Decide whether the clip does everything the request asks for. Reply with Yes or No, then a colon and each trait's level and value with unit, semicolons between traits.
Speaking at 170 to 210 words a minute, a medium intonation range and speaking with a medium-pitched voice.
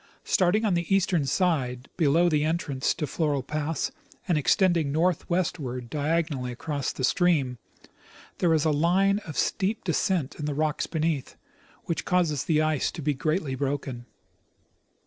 No: average, 150 wpm; average, 3.7 semitones; medium, 155 Hz